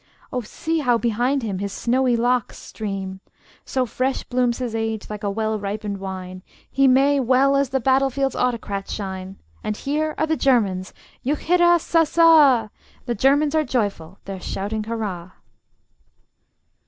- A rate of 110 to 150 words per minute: Yes, average, 145 wpm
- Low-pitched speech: No, high, 240 Hz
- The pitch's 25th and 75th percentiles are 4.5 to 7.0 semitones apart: Yes, average, 5.1 semitones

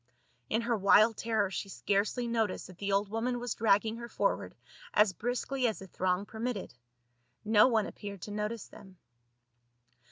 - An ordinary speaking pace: Yes, average, 160 wpm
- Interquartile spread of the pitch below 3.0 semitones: Yes, narrow, 2.6 semitones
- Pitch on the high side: Yes, high, 215 Hz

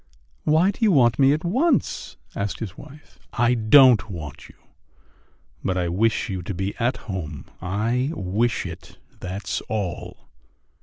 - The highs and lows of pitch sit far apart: Yes, wide, 6.2 semitones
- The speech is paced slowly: No, average, 150 wpm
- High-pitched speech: No, low, 110 Hz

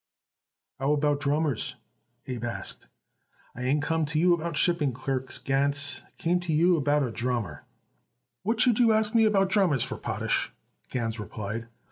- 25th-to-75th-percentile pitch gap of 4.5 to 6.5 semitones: Yes, average, 5.2 semitones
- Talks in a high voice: No, medium, 145 Hz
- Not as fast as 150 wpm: No, average, 170 wpm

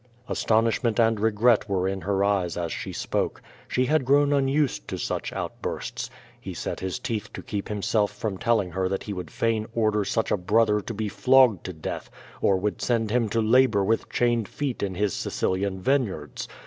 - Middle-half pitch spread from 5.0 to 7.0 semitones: No, average, 3.3 semitones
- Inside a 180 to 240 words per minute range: Yes, average, 190 wpm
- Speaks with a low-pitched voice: Yes, low, 105 Hz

